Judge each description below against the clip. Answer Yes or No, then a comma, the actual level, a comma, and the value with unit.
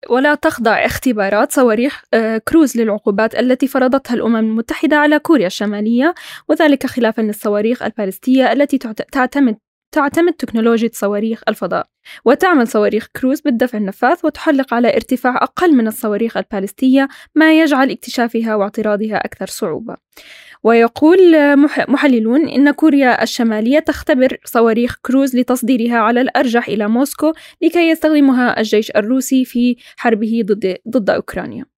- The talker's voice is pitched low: No, very high, 250 Hz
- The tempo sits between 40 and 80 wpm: No, average, 115 wpm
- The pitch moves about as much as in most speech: Yes, average, 4.4 semitones